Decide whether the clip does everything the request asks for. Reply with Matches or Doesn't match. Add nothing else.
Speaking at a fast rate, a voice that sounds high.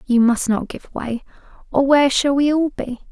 Matches